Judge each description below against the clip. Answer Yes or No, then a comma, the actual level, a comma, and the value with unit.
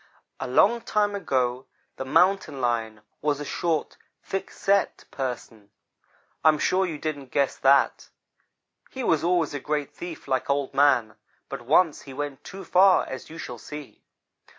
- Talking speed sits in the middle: Yes, average, 160 wpm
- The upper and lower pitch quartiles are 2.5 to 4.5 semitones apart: No, average, 5.1 semitones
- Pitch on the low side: No, medium, 145 Hz